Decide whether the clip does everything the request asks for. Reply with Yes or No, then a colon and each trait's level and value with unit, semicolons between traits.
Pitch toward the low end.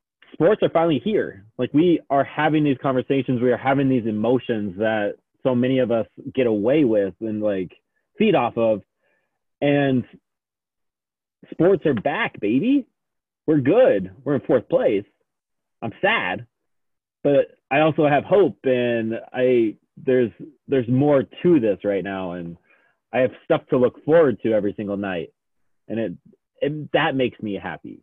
Yes: low, 125 Hz